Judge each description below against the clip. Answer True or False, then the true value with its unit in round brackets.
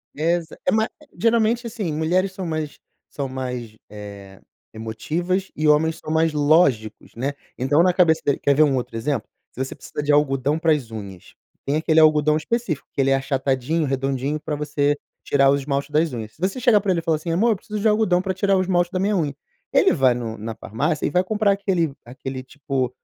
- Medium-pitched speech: True (150 Hz)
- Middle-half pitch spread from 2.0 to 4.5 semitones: False (4.9 semitones)